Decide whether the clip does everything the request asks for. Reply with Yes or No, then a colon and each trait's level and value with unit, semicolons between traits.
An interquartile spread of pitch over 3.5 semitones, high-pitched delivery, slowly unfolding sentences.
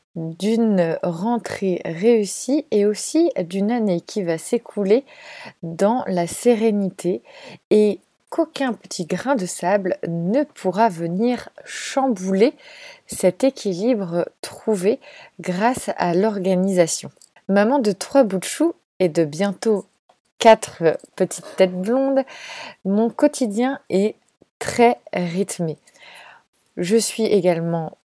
Yes: average, 4.8 semitones; high, 205 Hz; slow, 105 wpm